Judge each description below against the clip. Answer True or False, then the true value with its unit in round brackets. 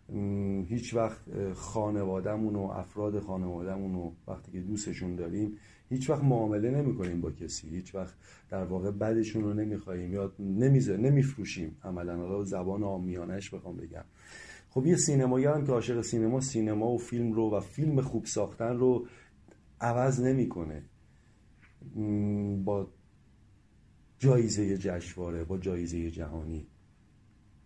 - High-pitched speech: False (100 Hz)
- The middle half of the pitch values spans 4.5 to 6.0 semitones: False (3.9 semitones)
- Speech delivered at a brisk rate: False (130 wpm)